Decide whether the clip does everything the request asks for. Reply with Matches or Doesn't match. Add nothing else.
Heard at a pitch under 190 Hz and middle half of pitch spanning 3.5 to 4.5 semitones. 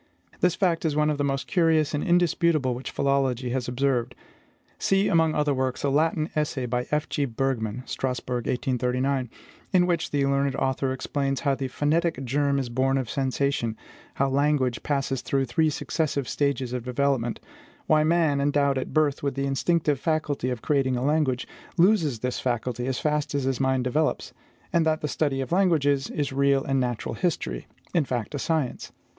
Doesn't match